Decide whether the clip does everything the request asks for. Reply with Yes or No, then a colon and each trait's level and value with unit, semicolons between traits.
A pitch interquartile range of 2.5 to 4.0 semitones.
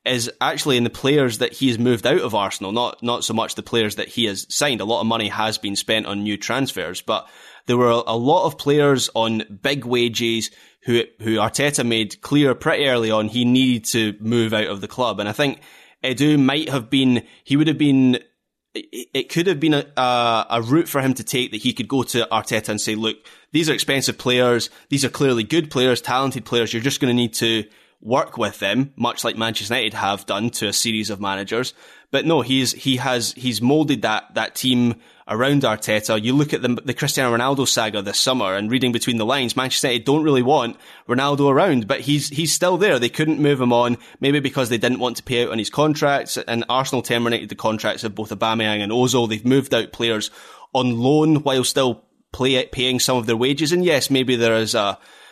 Yes: average, 3.1 semitones